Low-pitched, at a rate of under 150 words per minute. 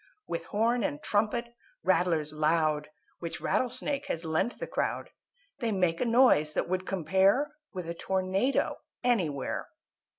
No: medium, 185 Hz; average, 140 wpm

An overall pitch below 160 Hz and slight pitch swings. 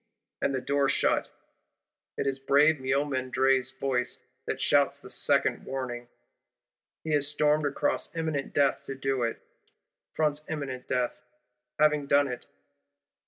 Yes: low, 135 Hz; narrow, 2.0 semitones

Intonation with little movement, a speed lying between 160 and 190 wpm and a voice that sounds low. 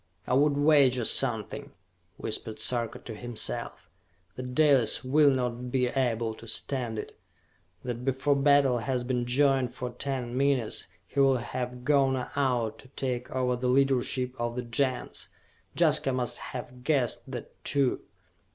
No: narrow, 1.9 semitones; average, 145 wpm; low, 125 Hz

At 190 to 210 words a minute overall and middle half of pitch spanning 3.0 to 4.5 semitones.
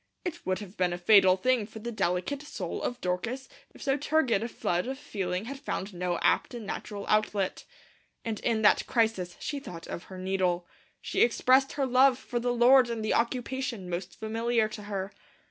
No: average, 195 wpm; average, 5.2 semitones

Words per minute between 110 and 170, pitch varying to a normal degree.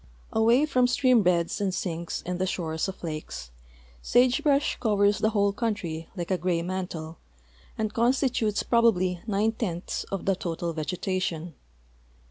Yes: average, 145 wpm; average, 4.8 semitones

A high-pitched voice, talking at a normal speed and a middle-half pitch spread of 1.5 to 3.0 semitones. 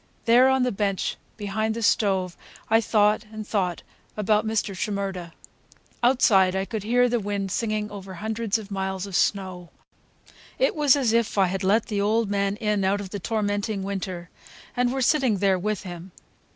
Yes: high, 205 Hz; average, 180 wpm; narrow, 2.5 semitones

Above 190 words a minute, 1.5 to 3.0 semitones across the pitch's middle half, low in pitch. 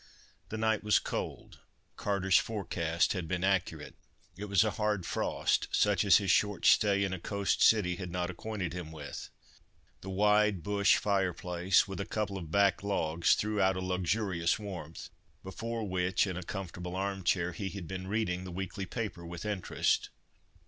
No: average, 170 wpm; narrow, 2.5 semitones; very low, 95 Hz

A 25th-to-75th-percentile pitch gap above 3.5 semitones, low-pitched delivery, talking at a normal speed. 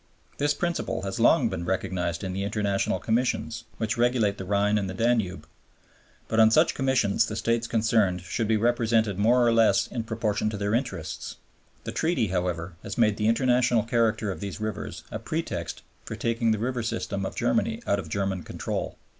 No: average, 3.0 semitones; low, 110 Hz; average, 185 wpm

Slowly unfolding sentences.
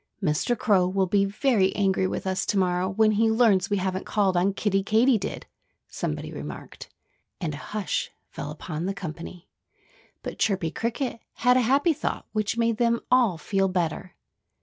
No: average, 170 wpm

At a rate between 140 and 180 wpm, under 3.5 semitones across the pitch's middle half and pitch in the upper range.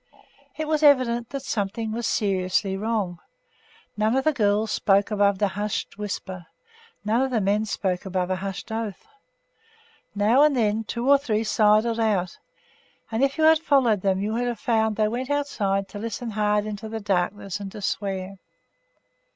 Yes: average, 175 wpm; average, 3.0 semitones; high, 215 Hz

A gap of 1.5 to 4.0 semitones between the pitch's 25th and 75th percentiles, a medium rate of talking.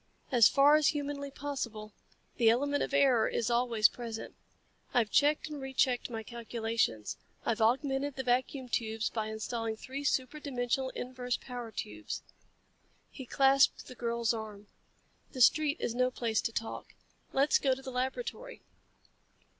Yes: average, 3.3 semitones; average, 150 wpm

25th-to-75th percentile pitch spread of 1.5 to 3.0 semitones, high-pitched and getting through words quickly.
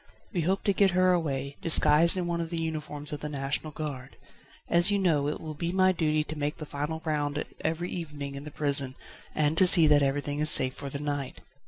No: average, 2.7 semitones; medium, 150 Hz; fast, 225 wpm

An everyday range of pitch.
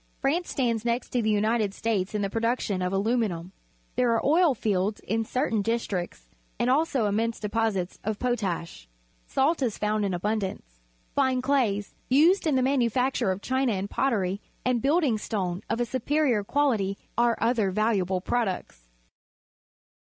Yes: average, 4.2 semitones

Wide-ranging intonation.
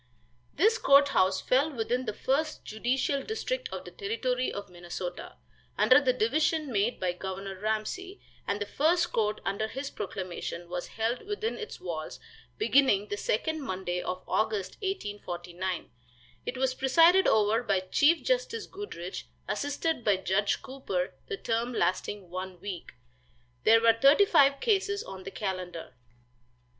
Yes: wide, 7.9 semitones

